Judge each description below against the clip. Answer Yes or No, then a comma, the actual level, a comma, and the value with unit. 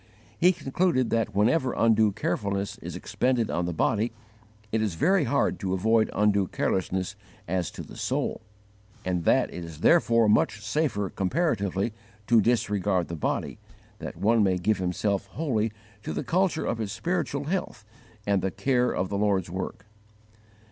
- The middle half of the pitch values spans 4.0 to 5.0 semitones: Yes, average, 4.5 semitones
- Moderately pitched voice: No, low, 105 Hz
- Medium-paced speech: Yes, average, 160 wpm